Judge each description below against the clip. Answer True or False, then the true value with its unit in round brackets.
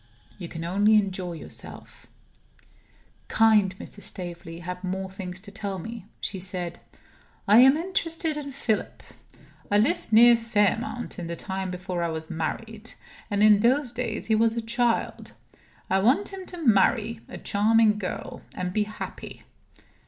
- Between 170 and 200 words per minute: False (150 wpm)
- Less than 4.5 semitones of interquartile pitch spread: True (3.9 semitones)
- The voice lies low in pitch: False (210 Hz)